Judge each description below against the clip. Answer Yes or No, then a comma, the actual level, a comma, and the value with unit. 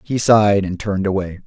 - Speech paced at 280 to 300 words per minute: No, fast, 205 wpm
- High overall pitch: No, low, 100 Hz